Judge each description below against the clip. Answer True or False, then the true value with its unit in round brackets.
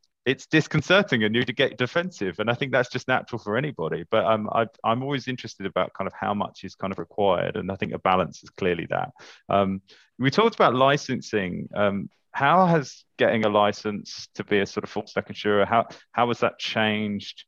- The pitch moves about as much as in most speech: True (4.5 semitones)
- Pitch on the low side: True (115 Hz)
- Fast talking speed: True (210 wpm)